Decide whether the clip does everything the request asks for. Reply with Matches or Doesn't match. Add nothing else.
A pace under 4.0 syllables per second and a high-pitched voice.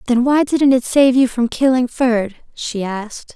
Doesn't match